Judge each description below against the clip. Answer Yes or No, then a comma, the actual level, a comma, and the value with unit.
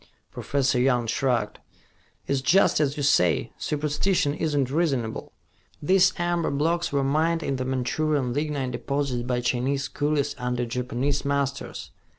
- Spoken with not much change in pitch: No, average, 3.2 semitones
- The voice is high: No, medium, 140 Hz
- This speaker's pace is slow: No, average, 145 wpm